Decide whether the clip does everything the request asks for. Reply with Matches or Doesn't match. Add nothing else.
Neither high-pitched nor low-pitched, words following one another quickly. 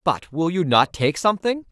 Matches